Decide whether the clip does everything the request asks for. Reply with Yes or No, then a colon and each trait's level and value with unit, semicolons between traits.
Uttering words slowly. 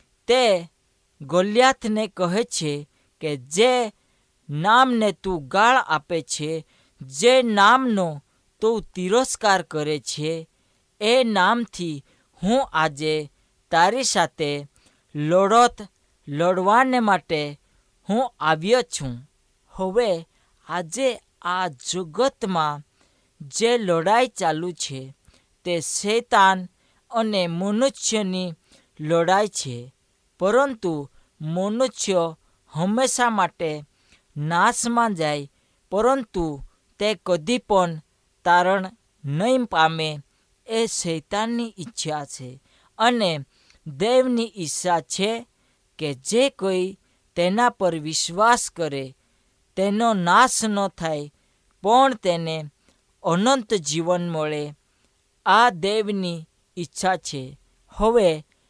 Yes: slow, 85 wpm